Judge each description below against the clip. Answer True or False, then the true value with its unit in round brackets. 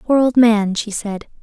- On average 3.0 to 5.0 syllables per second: True (4.1 syllables/s)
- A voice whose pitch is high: True (225 Hz)